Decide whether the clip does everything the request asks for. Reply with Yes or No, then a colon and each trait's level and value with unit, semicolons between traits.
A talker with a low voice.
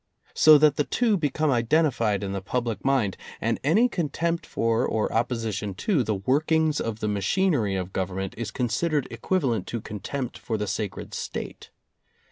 Yes: low, 120 Hz